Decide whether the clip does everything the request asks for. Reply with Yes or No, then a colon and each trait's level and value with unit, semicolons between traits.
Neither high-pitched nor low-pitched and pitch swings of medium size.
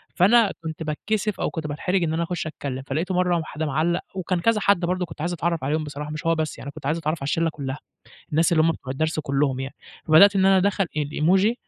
Yes: medium, 160 Hz; average, 3.3 semitones